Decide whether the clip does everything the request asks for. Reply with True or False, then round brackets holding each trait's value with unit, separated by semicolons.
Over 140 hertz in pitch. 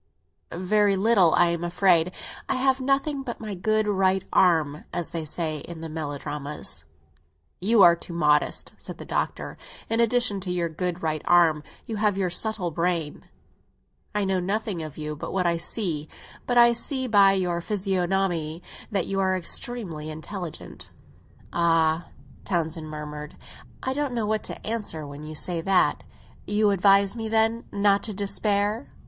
True (185 Hz)